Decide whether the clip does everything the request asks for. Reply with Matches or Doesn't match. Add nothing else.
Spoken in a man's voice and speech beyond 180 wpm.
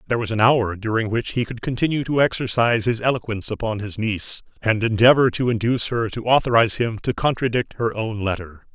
Matches